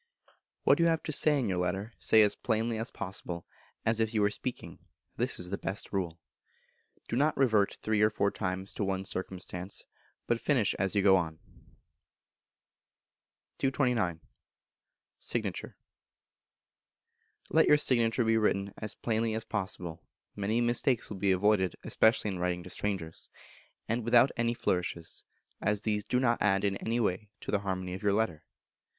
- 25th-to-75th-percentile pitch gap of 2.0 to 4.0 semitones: Yes, average, 3.6 semitones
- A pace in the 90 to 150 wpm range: No, average, 160 wpm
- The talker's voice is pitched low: Yes, low, 105 Hz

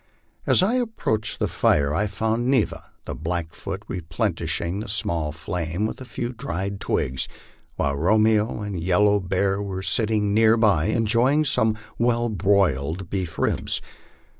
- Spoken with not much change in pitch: No, average, 4.2 semitones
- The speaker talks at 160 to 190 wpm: No, average, 145 wpm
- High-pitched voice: No, low, 100 Hz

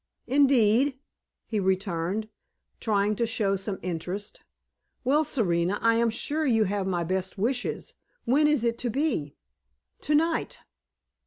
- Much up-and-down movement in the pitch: Yes, wide, 5.7 semitones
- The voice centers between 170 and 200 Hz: No, high, 220 Hz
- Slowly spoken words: Yes, slow, 130 wpm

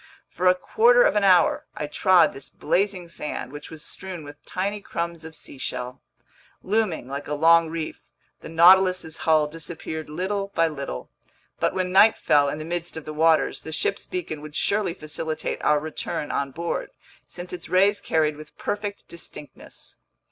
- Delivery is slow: No, average, 170 wpm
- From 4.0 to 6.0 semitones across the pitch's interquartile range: No, average, 3.4 semitones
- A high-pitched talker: No, medium, 165 Hz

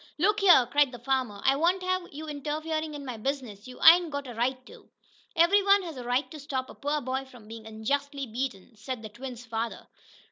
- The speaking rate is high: Yes, fast, 215 wpm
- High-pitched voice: Yes, very high, 270 Hz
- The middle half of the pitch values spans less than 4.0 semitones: No, average, 4.4 semitones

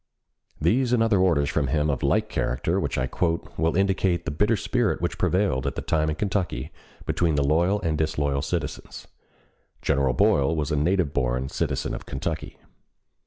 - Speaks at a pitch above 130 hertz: No, very low, 80 Hz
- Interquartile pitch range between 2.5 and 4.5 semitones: No, average, 5.0 semitones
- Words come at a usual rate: Yes, average, 175 wpm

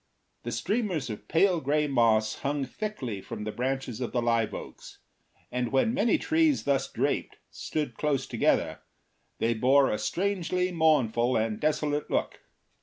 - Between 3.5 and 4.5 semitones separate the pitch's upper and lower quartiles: No, wide, 5.6 semitones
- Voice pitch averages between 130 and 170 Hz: Yes, low, 135 Hz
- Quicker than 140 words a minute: Yes, average, 150 wpm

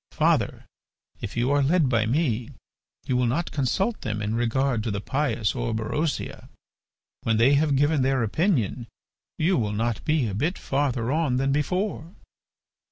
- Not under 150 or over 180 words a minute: Yes, average, 160 wpm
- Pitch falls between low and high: No, low, 130 Hz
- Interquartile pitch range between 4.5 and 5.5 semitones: Yes, average, 4.8 semitones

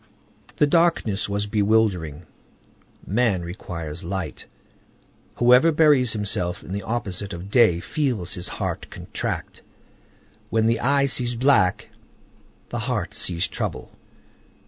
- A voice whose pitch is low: Yes, low, 105 Hz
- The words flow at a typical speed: No, slow, 115 wpm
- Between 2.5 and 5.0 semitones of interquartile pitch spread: No, wide, 5.6 semitones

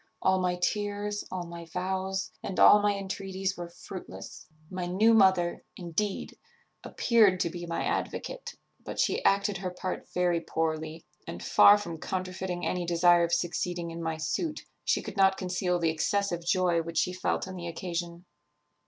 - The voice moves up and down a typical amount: No, narrow, 2.0 semitones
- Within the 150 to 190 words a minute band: Yes, average, 165 wpm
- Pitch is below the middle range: No, medium, 180 Hz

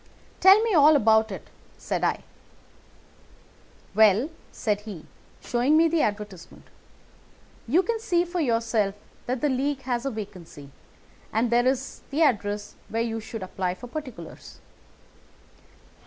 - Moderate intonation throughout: No, wide, 5.7 semitones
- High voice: Yes, high, 235 Hz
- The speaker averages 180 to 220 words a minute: No, slow, 135 wpm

